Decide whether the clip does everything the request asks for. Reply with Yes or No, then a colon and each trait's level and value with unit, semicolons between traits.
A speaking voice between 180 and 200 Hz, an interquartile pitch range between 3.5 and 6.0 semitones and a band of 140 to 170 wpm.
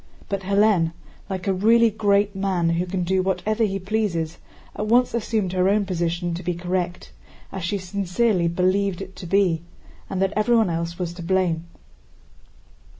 No: high, 190 Hz; narrow, 2.6 semitones; average, 165 wpm